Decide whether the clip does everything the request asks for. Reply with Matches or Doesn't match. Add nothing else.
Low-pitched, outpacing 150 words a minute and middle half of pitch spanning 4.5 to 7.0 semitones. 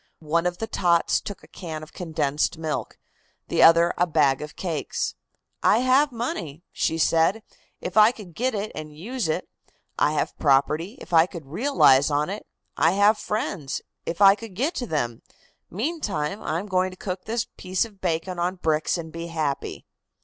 Doesn't match